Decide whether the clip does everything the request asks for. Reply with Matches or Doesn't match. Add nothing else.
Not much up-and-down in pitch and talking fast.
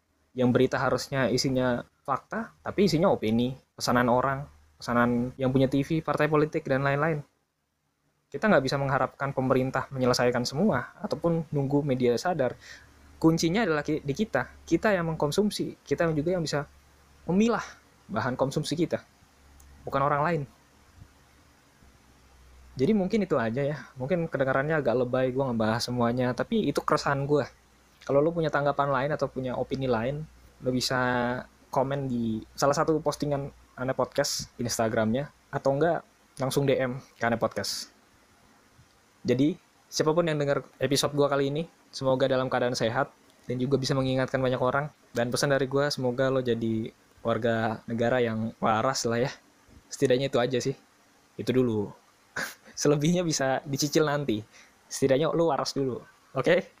Doesn't match